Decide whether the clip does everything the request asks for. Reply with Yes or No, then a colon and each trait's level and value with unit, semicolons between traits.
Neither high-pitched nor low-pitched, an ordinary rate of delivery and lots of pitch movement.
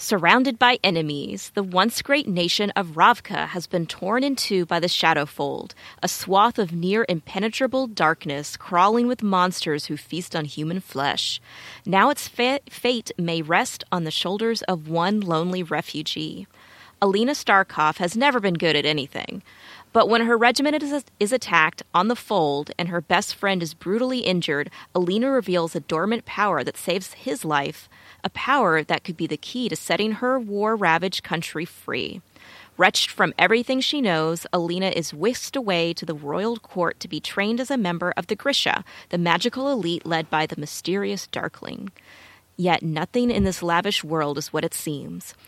Yes: medium, 180 Hz; average, 175 wpm; wide, 5.8 semitones